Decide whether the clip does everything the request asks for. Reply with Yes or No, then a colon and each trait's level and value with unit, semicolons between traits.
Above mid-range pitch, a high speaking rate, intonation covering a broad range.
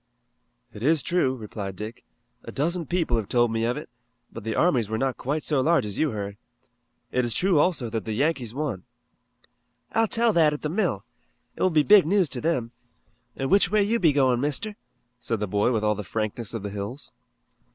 No: low, 130 Hz; fast, 210 wpm; wide, 6.8 semitones